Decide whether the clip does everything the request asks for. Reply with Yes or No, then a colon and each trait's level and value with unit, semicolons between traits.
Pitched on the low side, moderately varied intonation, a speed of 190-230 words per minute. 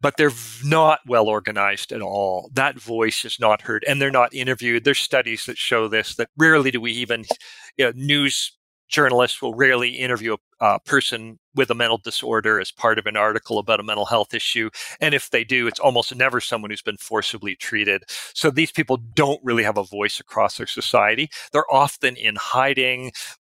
Yes: low, 120 Hz; average, 3.3 semitones; average, 195 wpm